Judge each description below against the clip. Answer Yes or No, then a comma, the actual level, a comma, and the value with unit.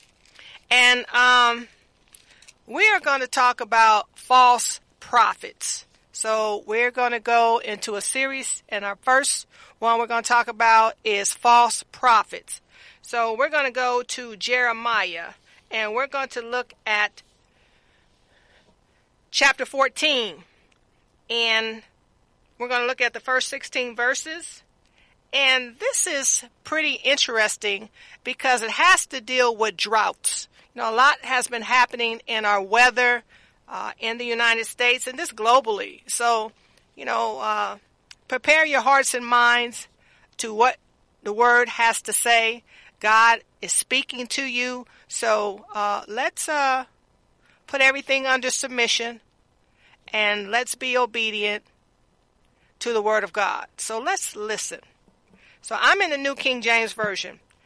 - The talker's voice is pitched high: Yes, high, 240 Hz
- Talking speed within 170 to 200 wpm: No, average, 140 wpm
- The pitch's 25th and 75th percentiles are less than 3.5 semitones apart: Yes, narrow, 2.5 semitones